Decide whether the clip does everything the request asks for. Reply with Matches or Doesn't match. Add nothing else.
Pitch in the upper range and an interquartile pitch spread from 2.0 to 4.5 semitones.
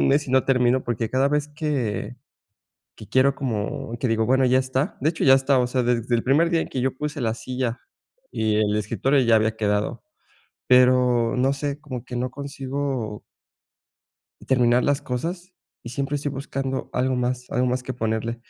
Doesn't match